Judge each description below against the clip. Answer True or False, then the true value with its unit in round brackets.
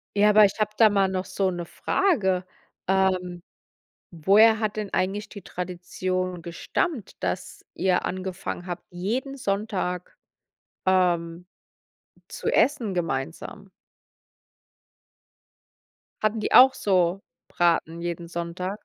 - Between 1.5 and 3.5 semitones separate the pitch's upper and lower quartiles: True (2.8 semitones)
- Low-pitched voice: False (185 Hz)